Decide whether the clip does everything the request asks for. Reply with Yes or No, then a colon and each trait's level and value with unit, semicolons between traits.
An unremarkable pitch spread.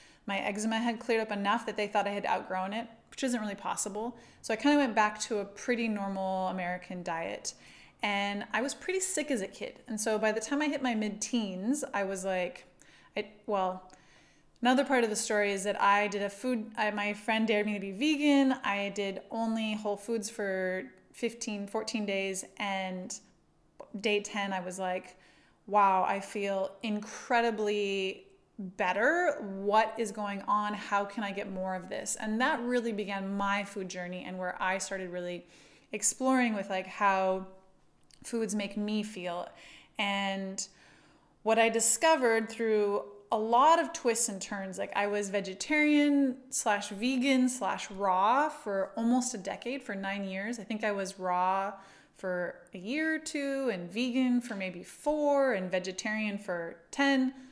Yes: average, 3.2 semitones